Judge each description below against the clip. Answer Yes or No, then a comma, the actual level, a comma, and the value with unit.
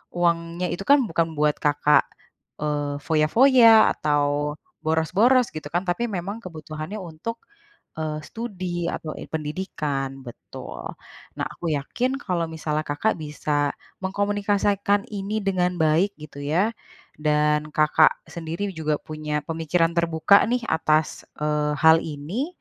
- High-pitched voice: No, medium, 160 Hz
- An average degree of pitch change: Yes, average, 4.5 semitones